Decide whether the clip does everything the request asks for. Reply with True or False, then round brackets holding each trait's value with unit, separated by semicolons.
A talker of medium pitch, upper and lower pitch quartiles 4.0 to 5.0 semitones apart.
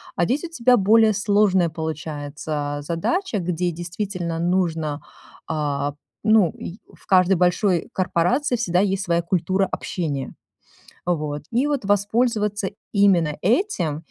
True (180 Hz; 4.4 semitones)